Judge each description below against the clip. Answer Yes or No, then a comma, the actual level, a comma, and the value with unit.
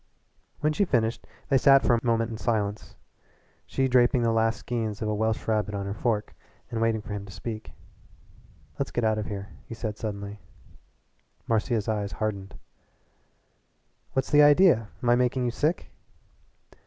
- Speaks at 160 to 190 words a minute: Yes, average, 165 wpm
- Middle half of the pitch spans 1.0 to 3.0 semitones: Yes, narrow, 2.6 semitones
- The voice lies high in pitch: No, low, 115 Hz